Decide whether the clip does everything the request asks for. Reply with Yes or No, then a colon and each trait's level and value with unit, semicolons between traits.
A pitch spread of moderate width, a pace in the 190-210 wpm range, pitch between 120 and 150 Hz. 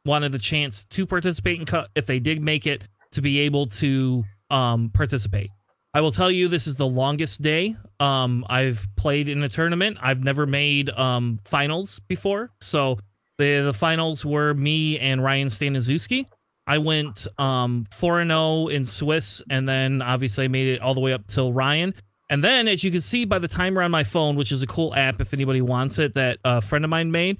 Yes: average, 3.4 semitones; fast, 205 wpm; medium, 140 Hz